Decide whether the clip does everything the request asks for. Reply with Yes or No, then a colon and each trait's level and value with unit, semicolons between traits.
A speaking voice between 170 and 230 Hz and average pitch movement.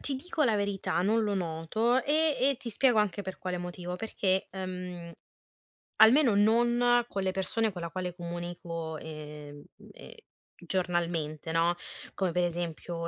Yes: medium, 185 Hz; average, 4.5 semitones